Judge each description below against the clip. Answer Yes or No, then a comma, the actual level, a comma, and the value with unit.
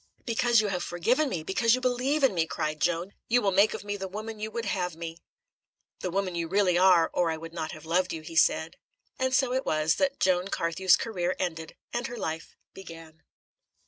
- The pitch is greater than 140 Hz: Yes, medium, 185 Hz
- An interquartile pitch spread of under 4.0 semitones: No, average, 5.3 semitones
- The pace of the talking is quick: Yes, fast, 215 wpm